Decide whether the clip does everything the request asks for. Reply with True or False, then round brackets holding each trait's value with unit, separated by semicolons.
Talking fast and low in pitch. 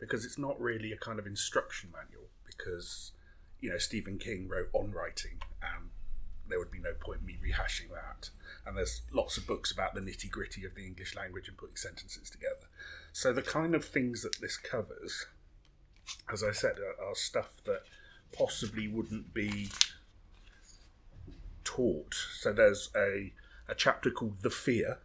False (170 wpm; 105 Hz)